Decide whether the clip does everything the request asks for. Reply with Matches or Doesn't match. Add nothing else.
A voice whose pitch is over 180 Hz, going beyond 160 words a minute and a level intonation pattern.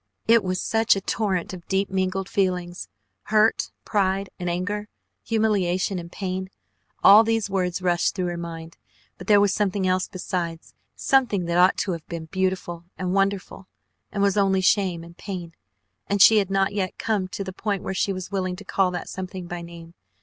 Matches